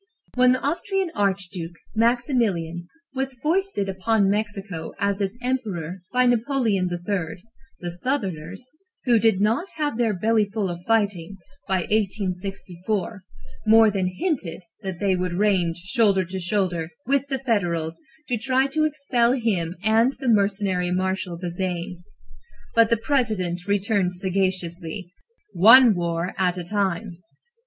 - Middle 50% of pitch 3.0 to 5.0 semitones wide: Yes, average, 4.5 semitones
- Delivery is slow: Yes, slow, 130 wpm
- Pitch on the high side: Yes, high, 200 Hz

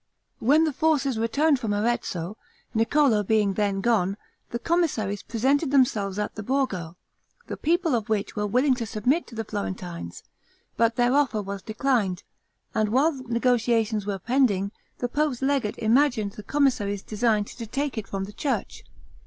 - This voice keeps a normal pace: Yes, average, 160 wpm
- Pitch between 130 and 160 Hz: No, high, 225 Hz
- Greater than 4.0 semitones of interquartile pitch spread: Yes, average, 4.6 semitones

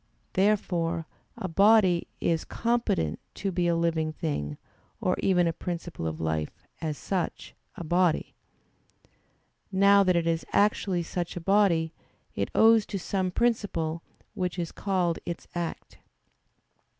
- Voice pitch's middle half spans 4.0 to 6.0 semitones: No, average, 3.0 semitones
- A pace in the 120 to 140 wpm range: Yes, slow, 135 wpm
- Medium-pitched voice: Yes, medium, 175 Hz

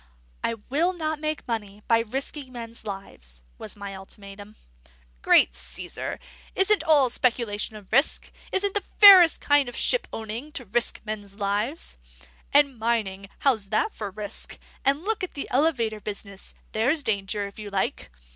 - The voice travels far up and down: Yes, wide, 6.1 semitones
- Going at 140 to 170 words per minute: Yes, average, 150 wpm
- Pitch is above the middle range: Yes, high, 230 Hz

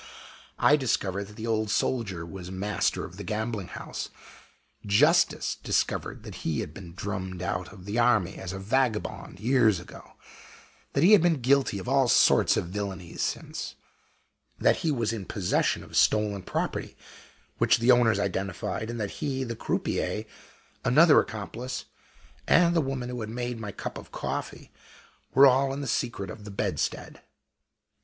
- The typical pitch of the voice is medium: No, low, 110 Hz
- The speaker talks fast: No, average, 165 wpm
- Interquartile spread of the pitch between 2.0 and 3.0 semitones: No, average, 4.7 semitones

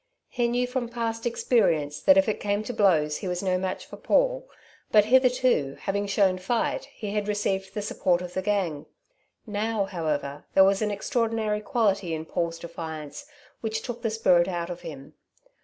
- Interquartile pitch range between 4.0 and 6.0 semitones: Yes, average, 4.5 semitones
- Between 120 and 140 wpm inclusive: No, average, 180 wpm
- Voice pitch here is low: No, high, 200 Hz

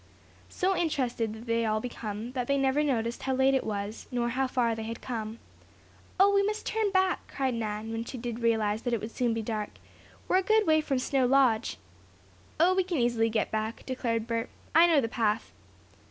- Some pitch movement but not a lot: Yes, average, 3.6 semitones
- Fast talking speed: Yes, fast, 210 wpm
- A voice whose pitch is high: Yes, high, 240 Hz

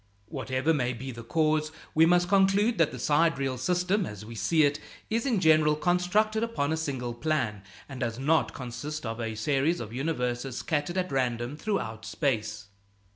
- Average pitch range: No, wide, 5.8 semitones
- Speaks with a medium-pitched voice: Yes, medium, 145 Hz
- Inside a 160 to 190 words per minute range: Yes, average, 175 wpm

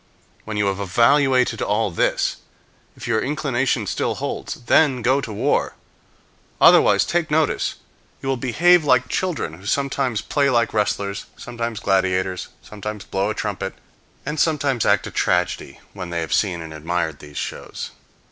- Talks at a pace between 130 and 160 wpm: Yes, average, 155 wpm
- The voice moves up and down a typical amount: No, wide, 5.8 semitones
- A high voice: No, low, 115 Hz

